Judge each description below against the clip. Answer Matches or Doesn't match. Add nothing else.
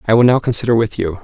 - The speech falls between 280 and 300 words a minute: Matches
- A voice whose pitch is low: Matches